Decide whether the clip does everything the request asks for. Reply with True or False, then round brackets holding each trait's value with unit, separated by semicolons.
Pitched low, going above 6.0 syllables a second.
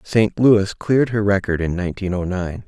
False (100 Hz; 5.1 syllables/s)